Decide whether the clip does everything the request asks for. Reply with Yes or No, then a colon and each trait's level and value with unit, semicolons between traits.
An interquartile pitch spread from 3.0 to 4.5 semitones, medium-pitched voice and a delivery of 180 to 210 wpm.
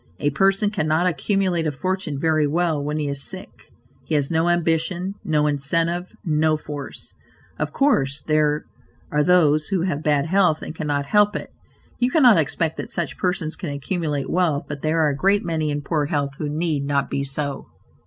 Yes: average, 3.3 semitones; medium, 155 Hz; average, 185 wpm